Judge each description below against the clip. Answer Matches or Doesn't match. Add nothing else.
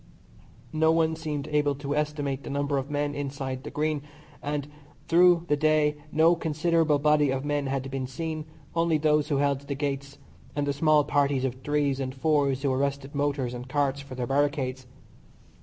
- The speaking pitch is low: Doesn't match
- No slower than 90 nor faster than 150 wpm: Doesn't match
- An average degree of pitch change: Doesn't match